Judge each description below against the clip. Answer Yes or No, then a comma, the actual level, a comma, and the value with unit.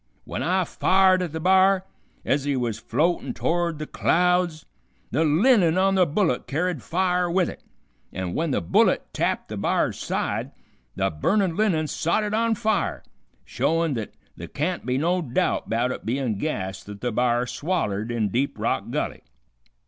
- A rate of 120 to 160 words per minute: No, average, 170 wpm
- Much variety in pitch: Yes, wide, 6.7 semitones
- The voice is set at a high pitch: No, medium, 160 Hz